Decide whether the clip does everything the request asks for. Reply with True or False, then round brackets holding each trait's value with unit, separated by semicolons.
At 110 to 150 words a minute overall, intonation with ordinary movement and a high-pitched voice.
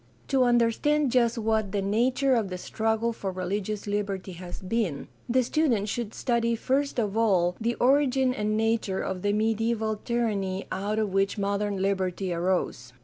False (160 wpm; 3.3 semitones; 215 Hz)